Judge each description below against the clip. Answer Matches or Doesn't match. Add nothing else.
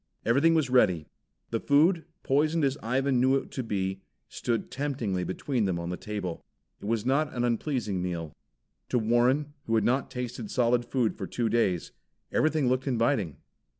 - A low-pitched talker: Matches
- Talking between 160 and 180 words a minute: Matches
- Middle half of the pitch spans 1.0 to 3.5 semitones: Doesn't match